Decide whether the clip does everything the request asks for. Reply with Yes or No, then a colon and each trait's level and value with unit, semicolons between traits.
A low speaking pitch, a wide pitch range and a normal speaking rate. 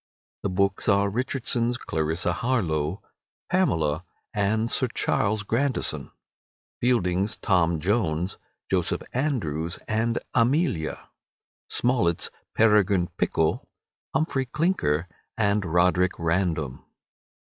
No: low, 100 Hz; wide, 5.8 semitones; slow, 90 wpm